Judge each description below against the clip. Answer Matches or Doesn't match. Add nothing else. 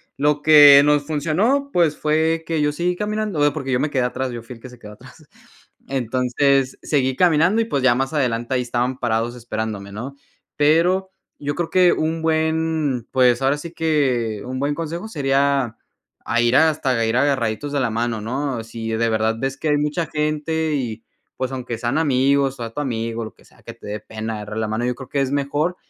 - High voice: Doesn't match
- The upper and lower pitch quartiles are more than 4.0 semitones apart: Matches